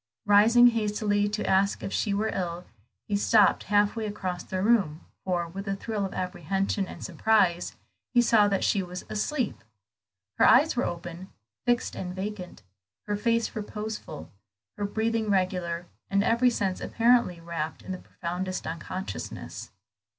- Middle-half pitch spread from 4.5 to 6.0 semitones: No, average, 3.1 semitones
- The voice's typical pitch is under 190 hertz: No, high, 200 Hz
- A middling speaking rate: Yes, average, 150 wpm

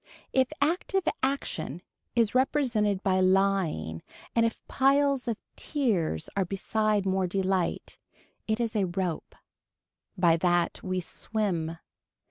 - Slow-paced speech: Yes, slow, 115 wpm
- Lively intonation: No, average, 4.7 semitones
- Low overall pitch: No, high, 195 Hz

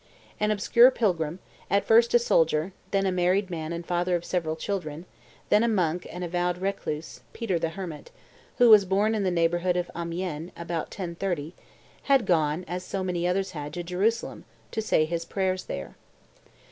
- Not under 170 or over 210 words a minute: Yes, average, 180 wpm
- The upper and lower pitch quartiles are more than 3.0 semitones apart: No, average, 2.7 semitones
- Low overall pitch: No, medium, 180 Hz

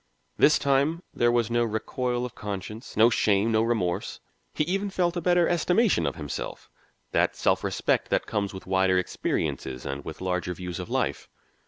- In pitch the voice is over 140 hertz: No, low, 115 Hz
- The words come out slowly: No, average, 175 wpm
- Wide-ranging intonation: Yes, wide, 7.8 semitones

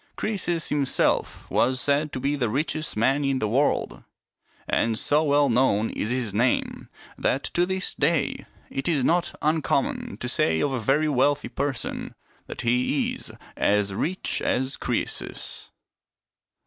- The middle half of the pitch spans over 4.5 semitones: No, average, 3.6 semitones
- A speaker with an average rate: Yes, average, 155 wpm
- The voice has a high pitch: No, low, 135 Hz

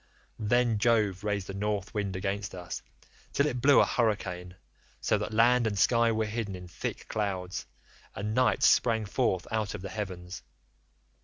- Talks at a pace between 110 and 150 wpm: No, average, 165 wpm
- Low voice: Yes, low, 105 Hz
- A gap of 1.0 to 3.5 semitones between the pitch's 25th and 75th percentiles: Yes, average, 3.1 semitones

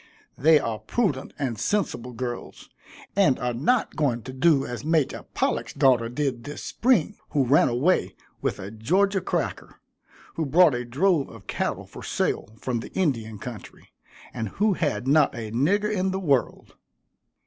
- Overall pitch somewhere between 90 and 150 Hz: Yes, low, 135 Hz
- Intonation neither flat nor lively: No, wide, 6.7 semitones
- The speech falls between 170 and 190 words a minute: No, average, 160 wpm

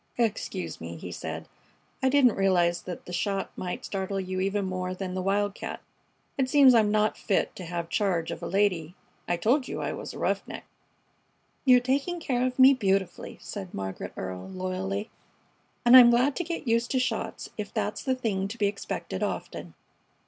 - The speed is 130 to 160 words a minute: No, average, 180 wpm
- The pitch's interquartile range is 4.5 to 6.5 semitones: Yes, average, 5.1 semitones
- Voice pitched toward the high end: Yes, high, 200 Hz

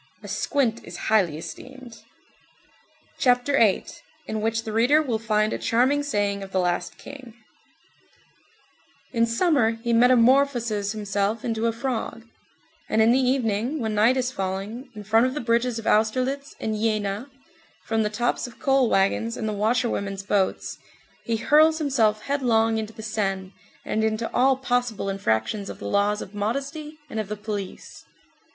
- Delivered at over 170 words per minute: No, average, 160 wpm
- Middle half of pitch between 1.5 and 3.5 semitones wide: Yes, average, 3.2 semitones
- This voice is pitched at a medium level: No, high, 225 Hz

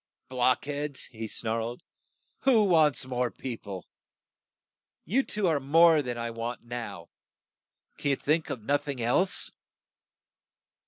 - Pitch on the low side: Yes, low, 130 Hz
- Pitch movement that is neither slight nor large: Yes, average, 4.5 semitones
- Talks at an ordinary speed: No, slow, 130 wpm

